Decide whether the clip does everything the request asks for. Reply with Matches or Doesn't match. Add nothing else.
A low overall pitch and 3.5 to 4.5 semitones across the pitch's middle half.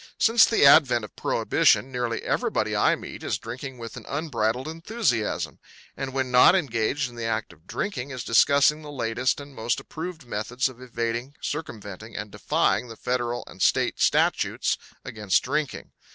Matches